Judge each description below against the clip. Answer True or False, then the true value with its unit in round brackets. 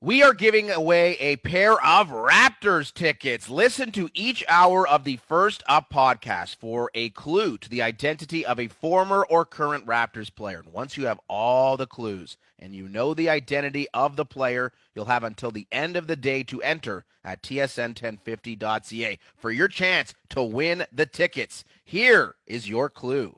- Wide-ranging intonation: True (6.9 semitones)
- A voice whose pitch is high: False (135 Hz)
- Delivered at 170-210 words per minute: True (175 wpm)